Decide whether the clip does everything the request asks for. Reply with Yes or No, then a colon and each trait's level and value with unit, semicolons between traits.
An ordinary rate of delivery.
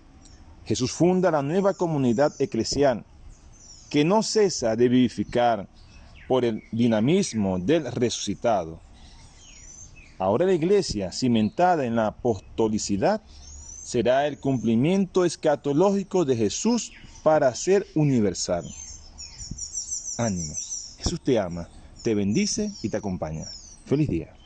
No: slow, 105 wpm